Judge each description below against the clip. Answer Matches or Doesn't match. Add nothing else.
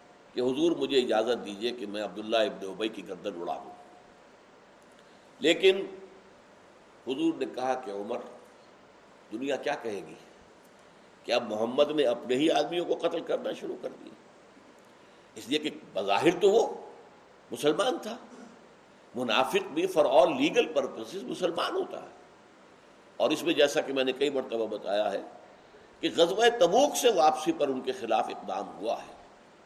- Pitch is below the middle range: Doesn't match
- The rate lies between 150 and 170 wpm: Matches